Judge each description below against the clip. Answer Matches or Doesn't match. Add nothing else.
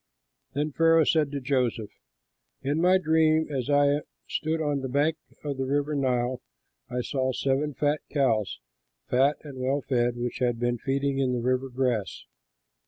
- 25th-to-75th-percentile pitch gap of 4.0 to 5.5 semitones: Doesn't match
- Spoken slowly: Doesn't match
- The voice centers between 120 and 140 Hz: Matches